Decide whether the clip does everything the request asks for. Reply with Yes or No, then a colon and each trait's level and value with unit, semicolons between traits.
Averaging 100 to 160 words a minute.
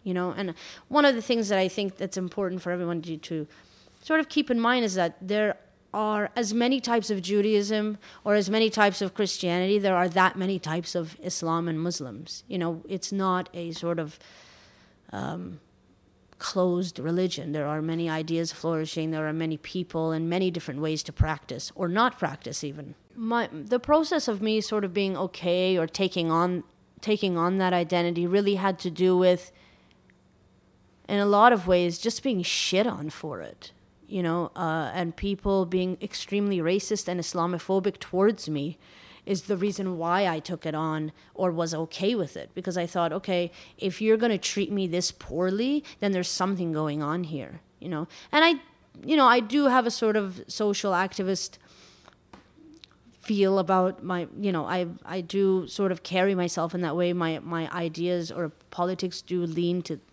No: average, 185 wpm